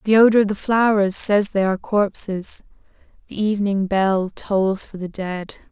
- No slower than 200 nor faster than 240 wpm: No, average, 170 wpm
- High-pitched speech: Yes, high, 200 Hz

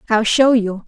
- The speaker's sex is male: No, female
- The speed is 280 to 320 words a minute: No, fast, 205 wpm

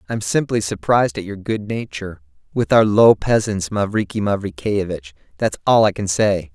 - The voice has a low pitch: Yes, low, 100 Hz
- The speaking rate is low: No, average, 165 wpm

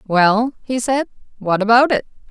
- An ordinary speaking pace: Yes, average, 155 wpm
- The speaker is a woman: Yes, female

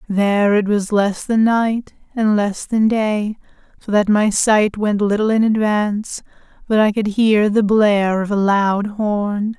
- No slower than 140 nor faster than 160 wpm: No, average, 175 wpm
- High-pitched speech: Yes, high, 210 Hz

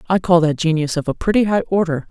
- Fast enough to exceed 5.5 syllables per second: Yes, 6.3 syllables/s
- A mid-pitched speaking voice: Yes, medium, 170 Hz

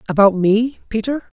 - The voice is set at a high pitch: Yes, high, 200 Hz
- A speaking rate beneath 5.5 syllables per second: Yes, 4.7 syllables/s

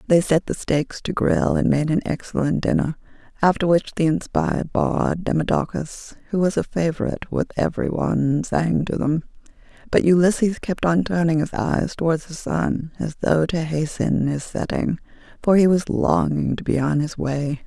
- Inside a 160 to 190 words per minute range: Yes, average, 175 wpm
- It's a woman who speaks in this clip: Yes, female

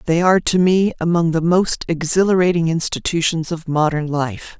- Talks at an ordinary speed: Yes, average, 155 wpm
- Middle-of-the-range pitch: Yes, medium, 165 Hz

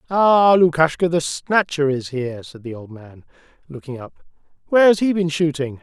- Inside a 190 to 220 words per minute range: No, average, 175 wpm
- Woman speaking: No, male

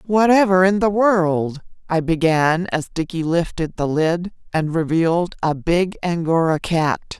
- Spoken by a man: No, female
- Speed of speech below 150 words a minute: Yes, average, 140 wpm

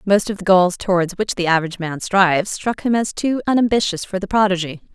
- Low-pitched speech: No, high, 190 Hz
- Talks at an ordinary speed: No, fast, 220 wpm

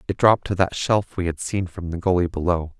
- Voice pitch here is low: Yes, very low, 90 Hz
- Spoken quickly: Yes, fast, 260 wpm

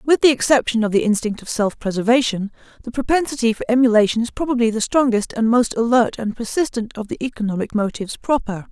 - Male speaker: No, female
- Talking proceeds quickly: No, average, 185 wpm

